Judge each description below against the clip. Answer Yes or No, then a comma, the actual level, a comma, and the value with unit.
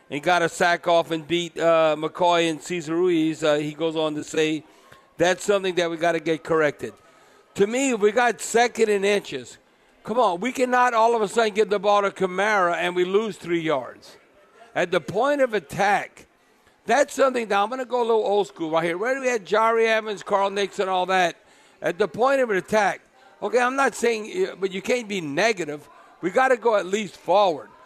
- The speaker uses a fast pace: Yes, fast, 220 wpm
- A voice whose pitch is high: Yes, high, 200 Hz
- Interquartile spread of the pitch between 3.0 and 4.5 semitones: No, average, 5.0 semitones